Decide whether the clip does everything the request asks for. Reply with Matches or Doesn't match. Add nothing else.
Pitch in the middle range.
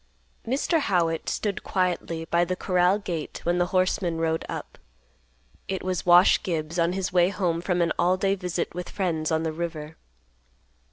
Matches